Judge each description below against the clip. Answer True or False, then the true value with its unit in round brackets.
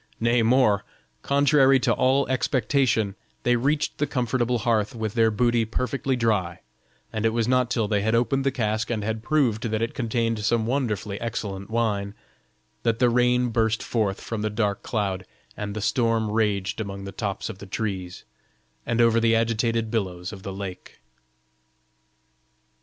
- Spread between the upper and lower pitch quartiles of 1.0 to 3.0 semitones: True (2.7 semitones)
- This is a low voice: True (115 Hz)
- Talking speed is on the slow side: False (165 wpm)